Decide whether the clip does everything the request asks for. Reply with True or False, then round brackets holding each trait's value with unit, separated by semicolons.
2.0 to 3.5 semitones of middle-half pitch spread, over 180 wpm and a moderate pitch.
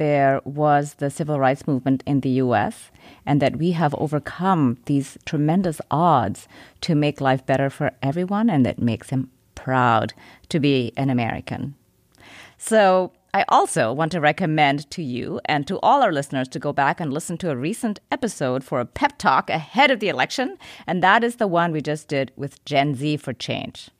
False (4.0 semitones; 190 wpm; 145 Hz)